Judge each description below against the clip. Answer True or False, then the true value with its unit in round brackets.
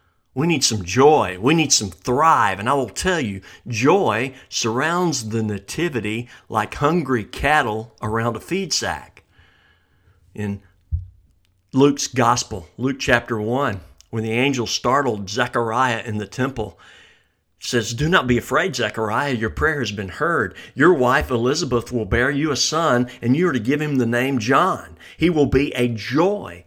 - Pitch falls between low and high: False (120 Hz)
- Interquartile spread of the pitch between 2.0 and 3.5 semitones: False (4.1 semitones)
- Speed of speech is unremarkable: True (160 wpm)